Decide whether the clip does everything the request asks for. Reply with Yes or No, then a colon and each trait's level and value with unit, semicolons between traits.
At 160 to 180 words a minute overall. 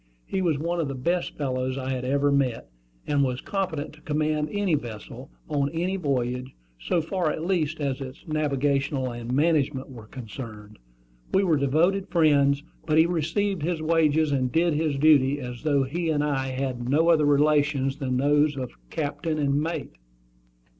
Yes: average, 175 wpm